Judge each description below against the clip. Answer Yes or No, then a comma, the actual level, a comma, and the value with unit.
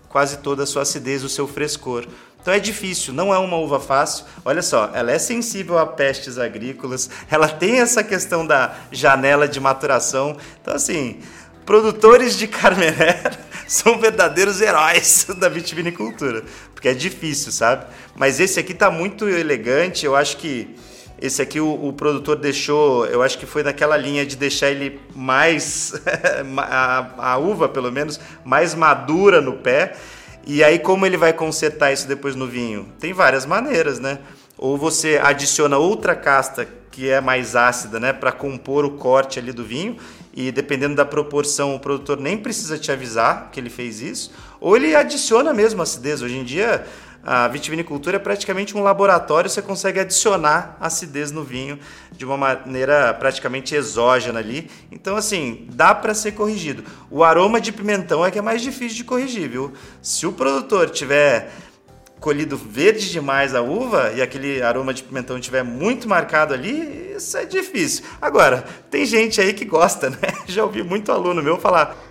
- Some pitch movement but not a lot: No, wide, 6.2 semitones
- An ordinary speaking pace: Yes, average, 170 wpm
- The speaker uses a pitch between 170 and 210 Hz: No, medium, 150 Hz